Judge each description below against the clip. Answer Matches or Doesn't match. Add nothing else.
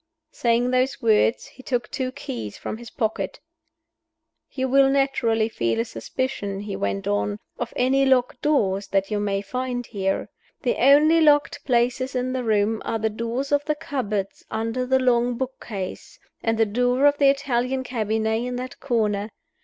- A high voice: Matches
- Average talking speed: Matches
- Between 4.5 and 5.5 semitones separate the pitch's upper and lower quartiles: Doesn't match